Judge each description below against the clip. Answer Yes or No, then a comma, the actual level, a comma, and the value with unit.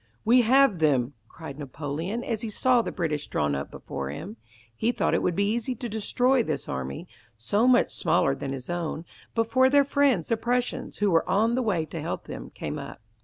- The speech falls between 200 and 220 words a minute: Yes, fast, 205 wpm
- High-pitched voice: Yes, high, 205 Hz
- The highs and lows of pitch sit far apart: Yes, wide, 8.7 semitones